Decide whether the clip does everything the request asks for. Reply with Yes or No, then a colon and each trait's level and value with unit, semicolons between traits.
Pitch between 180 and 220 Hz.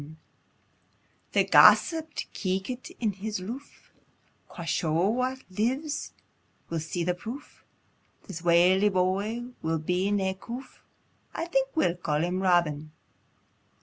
Yes: high, 190 Hz